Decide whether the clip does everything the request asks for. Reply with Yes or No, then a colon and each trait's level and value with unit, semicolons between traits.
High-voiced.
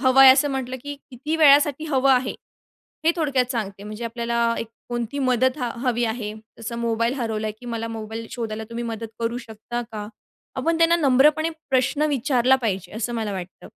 Yes: high, 240 Hz